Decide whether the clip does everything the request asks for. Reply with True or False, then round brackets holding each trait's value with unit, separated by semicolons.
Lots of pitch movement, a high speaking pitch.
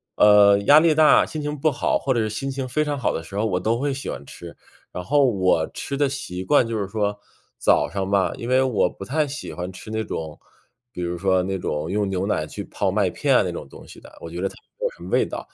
False (6.8 semitones; 105 Hz)